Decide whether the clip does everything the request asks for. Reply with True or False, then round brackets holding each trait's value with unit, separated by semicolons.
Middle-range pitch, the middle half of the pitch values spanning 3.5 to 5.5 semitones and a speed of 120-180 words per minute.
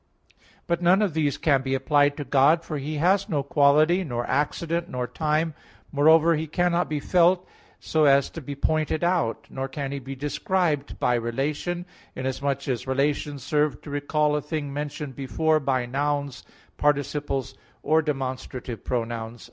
False (145 Hz; 2.7 semitones; 160 wpm)